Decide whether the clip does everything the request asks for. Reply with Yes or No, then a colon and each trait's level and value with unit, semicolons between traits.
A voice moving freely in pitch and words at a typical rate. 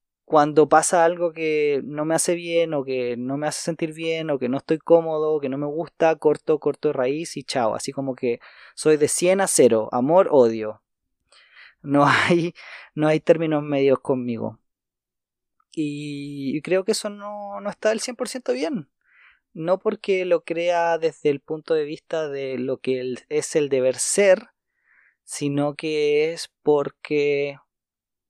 No: average, 3.4 semitones; average, 165 wpm